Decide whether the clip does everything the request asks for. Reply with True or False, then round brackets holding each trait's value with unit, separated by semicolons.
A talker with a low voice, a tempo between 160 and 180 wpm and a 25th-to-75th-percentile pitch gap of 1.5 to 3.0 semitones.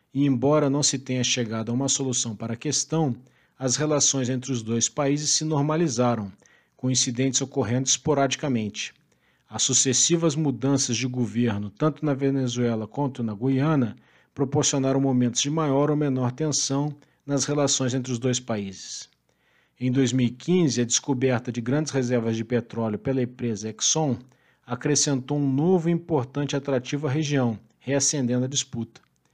False (130 Hz; 145 wpm; 2.7 semitones)